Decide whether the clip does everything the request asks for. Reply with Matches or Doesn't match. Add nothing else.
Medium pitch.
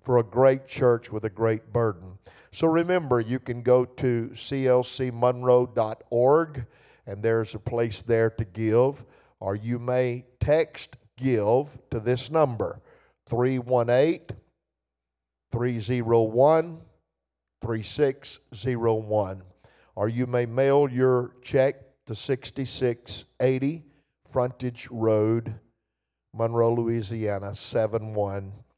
Doesn't match